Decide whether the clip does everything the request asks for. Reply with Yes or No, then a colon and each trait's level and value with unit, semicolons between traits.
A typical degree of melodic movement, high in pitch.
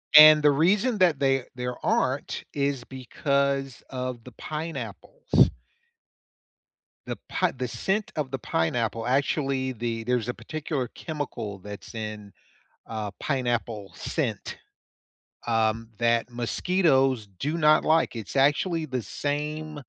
No: average, 4.5 semitones; low, 135 Hz